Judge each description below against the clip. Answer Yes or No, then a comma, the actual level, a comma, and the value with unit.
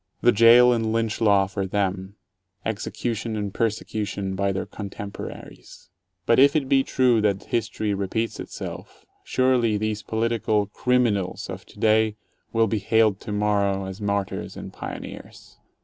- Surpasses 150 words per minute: No, average, 140 wpm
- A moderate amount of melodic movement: No, narrow, 2.3 semitones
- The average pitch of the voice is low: Yes, low, 110 Hz